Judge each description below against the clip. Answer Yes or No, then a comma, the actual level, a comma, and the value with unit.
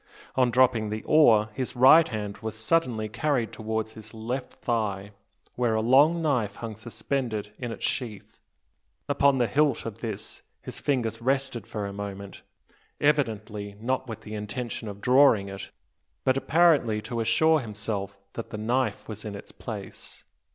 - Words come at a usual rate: Yes, average, 160 wpm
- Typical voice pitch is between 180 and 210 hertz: No, low, 115 Hz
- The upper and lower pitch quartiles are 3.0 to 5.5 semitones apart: Yes, average, 3.5 semitones